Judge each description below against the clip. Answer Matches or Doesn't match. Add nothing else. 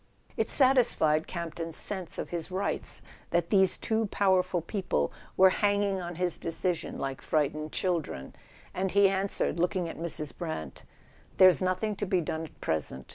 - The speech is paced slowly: Doesn't match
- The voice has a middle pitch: Matches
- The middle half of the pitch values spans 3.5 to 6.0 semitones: Doesn't match